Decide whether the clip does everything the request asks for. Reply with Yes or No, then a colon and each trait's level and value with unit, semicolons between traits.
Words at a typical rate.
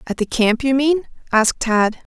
Yes: average, 190 wpm